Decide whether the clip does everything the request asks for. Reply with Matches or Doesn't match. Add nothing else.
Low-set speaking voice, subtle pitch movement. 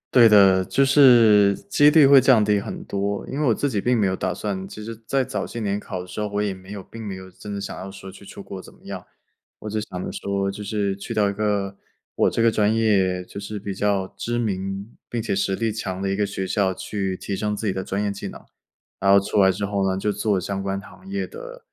Matches